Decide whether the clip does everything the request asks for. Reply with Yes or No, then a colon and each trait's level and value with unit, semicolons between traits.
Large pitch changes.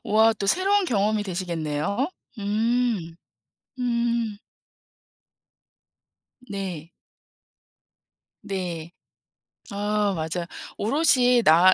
No: average, 4.9 semitones